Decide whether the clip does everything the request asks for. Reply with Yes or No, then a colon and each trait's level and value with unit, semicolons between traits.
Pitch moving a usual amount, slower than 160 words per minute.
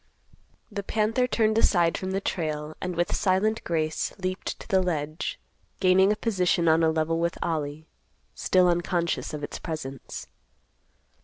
Yes: average, 3.2 semitones; average, 145 wpm